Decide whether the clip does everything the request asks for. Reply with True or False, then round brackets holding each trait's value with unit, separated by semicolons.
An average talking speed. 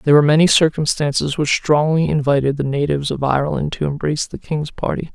True (185 wpm)